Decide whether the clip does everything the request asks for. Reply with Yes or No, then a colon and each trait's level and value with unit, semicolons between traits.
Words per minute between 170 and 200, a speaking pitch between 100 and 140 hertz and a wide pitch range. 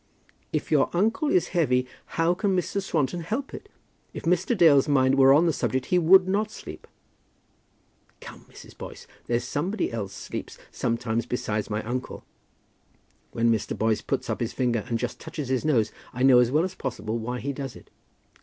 Yes: average, 180 wpm; low, 135 Hz; wide, 6.6 semitones